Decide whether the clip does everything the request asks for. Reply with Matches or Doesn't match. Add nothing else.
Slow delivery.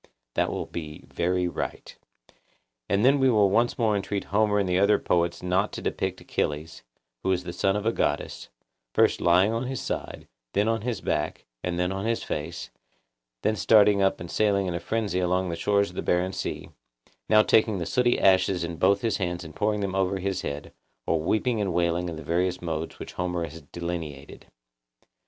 Doesn't match